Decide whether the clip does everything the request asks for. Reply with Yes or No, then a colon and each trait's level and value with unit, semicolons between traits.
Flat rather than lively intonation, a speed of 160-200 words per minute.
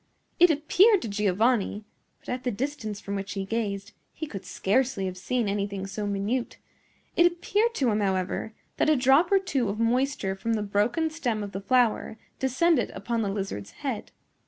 No: average, 5.0 semitones; average, 175 wpm